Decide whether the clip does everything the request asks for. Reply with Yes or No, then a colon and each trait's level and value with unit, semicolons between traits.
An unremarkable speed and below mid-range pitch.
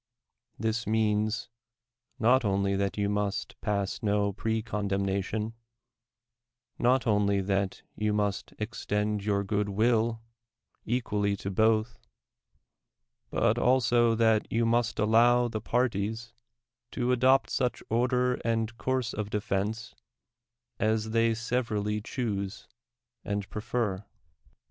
No: slow, 110 wpm; low, 110 Hz